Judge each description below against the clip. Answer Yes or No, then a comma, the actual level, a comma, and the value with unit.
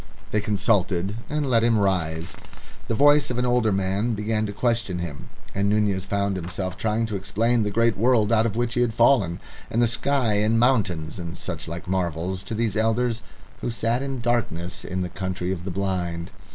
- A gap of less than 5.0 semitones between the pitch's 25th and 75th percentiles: Yes, average, 4.0 semitones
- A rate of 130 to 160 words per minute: No, fast, 205 wpm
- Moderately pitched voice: No, low, 105 Hz